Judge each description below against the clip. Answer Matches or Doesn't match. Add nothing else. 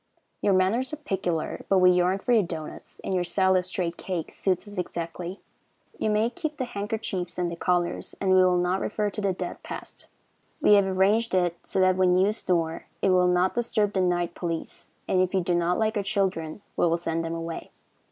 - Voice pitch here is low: Doesn't match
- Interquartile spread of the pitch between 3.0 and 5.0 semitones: Doesn't match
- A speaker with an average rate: Doesn't match